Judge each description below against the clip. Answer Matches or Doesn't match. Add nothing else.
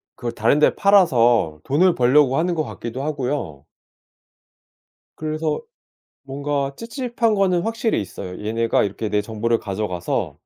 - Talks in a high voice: Doesn't match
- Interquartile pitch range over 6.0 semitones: Matches